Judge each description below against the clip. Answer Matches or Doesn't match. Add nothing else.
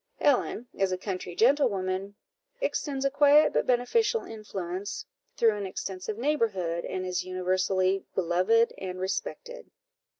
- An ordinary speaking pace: Doesn't match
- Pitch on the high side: Matches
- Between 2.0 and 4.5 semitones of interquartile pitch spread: Doesn't match